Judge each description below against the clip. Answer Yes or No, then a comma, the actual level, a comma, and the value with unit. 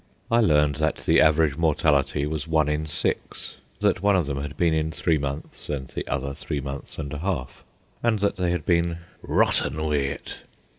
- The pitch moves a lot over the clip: No, average, 2.8 semitones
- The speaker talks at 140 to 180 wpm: No, average, 195 wpm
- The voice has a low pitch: Yes, very low, 75 Hz